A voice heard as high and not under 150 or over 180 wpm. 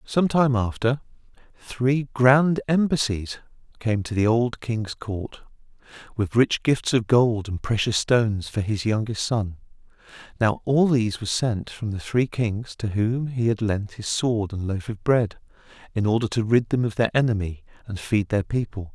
No: low, 115 Hz; average, 175 wpm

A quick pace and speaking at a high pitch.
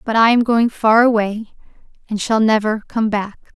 No: average, 185 wpm; high, 220 Hz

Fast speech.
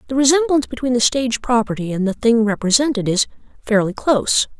No: average, 170 wpm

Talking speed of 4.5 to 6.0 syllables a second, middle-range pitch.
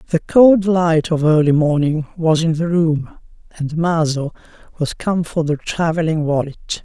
No: 4.3 syllables/s; medium, 160 Hz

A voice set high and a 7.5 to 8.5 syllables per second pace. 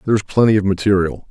No: low, 100 Hz; 7.7 syllables/s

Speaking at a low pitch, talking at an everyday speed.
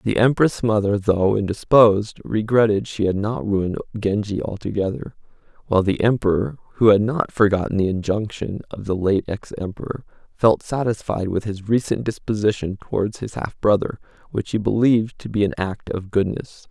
Yes: low, 105 Hz; average, 160 wpm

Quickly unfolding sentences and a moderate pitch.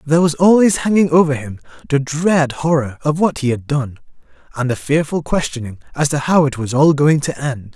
Yes: fast, 210 wpm; medium, 145 Hz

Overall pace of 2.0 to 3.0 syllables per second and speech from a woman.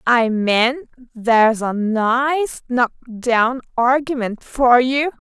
Yes: 2.8 syllables/s; female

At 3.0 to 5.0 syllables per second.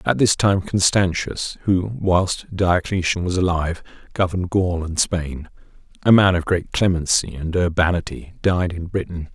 Yes: 4.5 syllables/s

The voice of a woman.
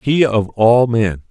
No: male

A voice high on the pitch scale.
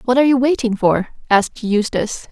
Yes: high, 235 Hz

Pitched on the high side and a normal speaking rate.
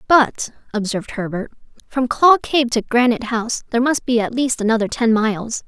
Yes: high, 235 Hz; average, 180 wpm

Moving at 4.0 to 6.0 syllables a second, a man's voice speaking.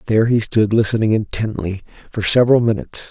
No: 6.4 syllables/s; male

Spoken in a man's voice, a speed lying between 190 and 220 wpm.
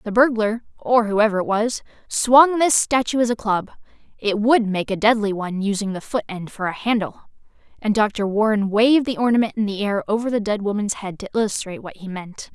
No: female; average, 200 wpm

